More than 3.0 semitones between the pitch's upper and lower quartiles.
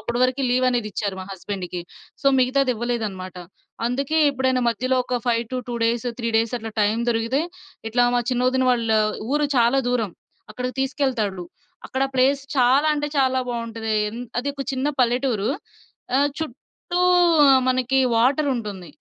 No: narrow, 2.5 semitones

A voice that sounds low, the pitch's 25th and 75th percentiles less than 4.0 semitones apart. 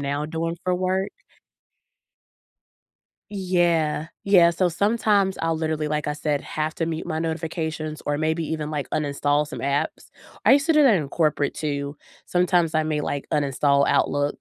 No: medium, 160 Hz; average, 2.9 semitones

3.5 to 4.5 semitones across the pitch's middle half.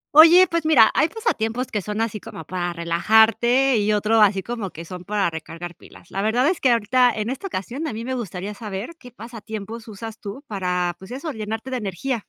Yes: average, 4.2 semitones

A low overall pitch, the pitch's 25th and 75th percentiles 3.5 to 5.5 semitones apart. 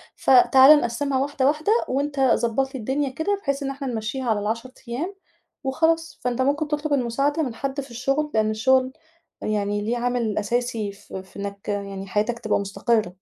No: very high, 255 Hz; average, 4.3 semitones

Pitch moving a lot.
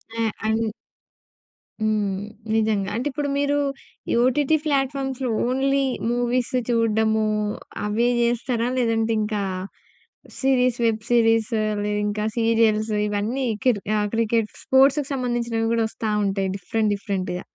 No: average, 2.8 semitones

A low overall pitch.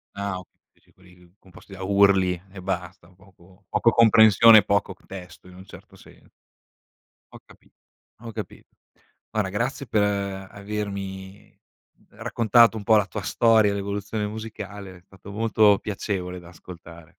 Yes: low, 100 Hz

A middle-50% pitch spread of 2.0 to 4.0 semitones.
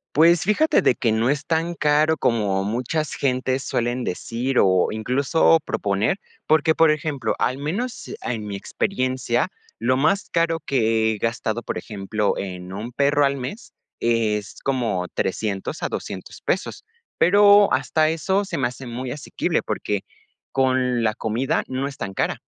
No: wide, 5.6 semitones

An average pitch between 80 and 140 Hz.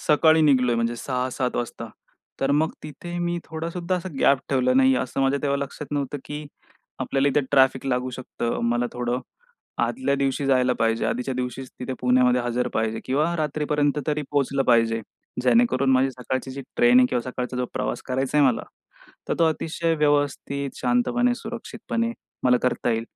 Yes: low, 135 Hz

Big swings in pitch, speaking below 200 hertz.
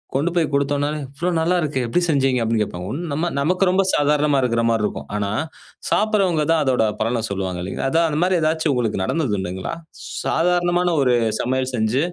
Yes: wide, 6.2 semitones; medium, 140 Hz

